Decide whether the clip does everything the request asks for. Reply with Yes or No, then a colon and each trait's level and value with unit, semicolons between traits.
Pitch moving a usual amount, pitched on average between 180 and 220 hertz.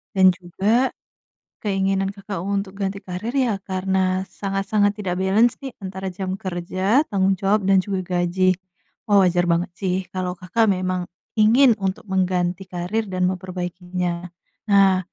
No: narrow, 1.6 semitones; high, 190 Hz